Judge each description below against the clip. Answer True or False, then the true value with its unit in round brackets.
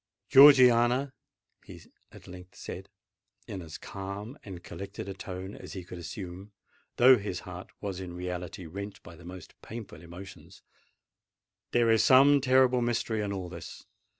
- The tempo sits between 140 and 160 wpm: True (150 wpm)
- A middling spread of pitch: True (4.7 semitones)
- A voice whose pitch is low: True (100 Hz)